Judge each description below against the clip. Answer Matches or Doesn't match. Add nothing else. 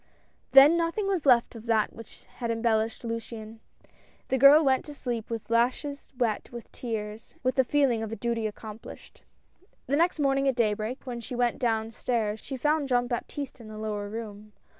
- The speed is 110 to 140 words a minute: Doesn't match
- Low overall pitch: Doesn't match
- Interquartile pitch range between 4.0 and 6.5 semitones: Doesn't match